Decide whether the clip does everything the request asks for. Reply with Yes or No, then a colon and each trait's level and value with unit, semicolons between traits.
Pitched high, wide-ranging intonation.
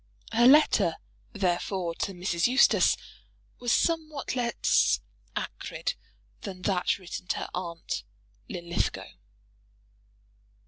Yes: high, 195 Hz; wide, 5.7 semitones